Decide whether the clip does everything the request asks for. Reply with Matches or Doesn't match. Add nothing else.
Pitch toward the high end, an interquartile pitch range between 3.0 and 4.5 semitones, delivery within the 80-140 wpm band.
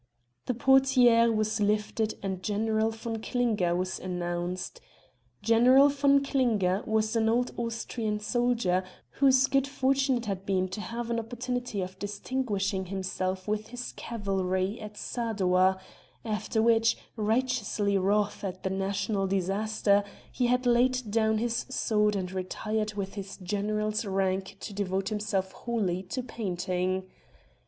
Matches